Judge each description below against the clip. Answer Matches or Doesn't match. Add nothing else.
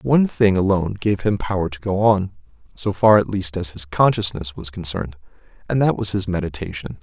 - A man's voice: Matches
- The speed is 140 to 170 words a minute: Doesn't match